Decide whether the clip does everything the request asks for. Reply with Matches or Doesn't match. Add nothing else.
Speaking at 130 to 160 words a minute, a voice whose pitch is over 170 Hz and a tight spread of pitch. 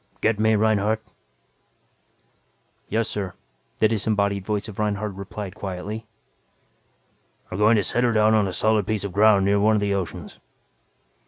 Doesn't match